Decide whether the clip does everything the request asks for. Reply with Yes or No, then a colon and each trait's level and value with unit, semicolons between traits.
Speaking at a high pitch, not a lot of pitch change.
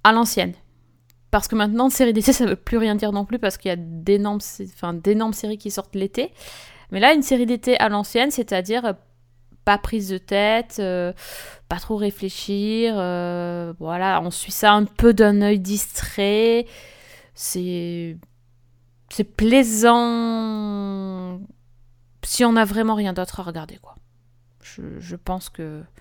No: high, 200 Hz; average, 4.1 semitones